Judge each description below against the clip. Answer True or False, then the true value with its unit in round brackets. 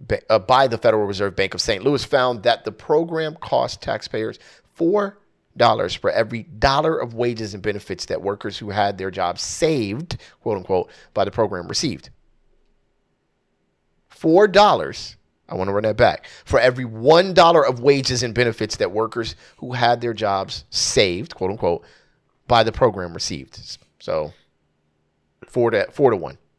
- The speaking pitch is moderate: False (115 Hz)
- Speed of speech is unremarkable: True (160 wpm)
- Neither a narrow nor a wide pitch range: True (4.4 semitones)